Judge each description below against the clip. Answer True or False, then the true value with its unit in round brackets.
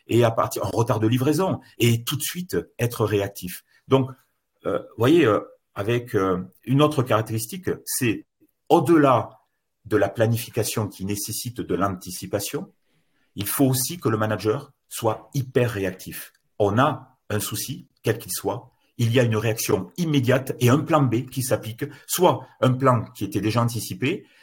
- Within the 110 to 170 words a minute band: True (165 wpm)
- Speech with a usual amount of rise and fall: True (4.0 semitones)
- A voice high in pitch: False (120 Hz)